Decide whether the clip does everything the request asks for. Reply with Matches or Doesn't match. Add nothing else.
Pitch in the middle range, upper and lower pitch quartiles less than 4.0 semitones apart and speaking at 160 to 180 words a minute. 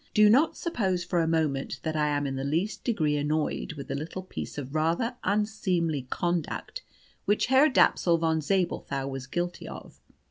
Doesn't match